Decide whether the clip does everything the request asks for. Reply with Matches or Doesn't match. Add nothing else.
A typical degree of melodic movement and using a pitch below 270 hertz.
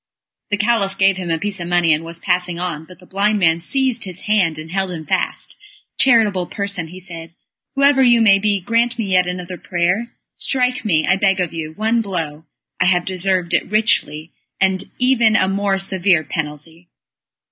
Matches